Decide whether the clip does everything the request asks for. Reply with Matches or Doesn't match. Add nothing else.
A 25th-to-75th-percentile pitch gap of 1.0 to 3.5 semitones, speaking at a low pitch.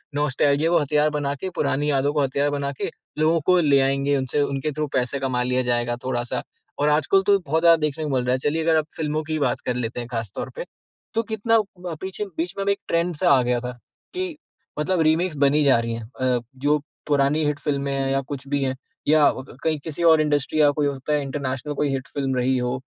Doesn't match